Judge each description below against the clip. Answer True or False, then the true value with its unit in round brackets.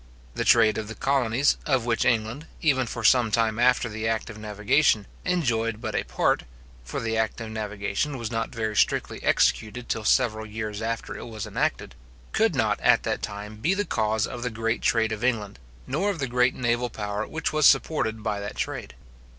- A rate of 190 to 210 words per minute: True (200 wpm)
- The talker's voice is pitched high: False (115 Hz)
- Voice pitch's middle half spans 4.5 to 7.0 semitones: False (2.4 semitones)